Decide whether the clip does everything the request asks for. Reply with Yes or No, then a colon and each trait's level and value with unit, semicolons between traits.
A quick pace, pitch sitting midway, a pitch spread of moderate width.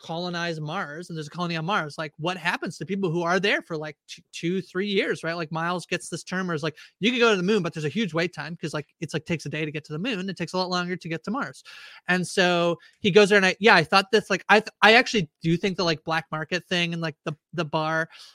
Yes: fast, 300 wpm; medium, 175 Hz; average, 3.1 semitones